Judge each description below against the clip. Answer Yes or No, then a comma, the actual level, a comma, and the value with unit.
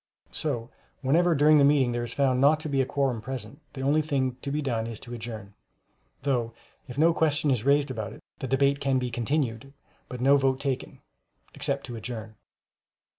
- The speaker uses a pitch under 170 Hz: Yes, low, 135 Hz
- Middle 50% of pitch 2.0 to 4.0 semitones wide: Yes, average, 3.0 semitones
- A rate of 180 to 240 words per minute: Yes, average, 190 wpm